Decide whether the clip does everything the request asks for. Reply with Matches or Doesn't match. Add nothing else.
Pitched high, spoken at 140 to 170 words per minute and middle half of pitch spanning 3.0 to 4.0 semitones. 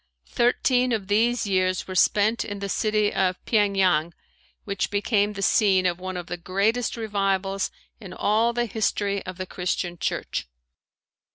Doesn't match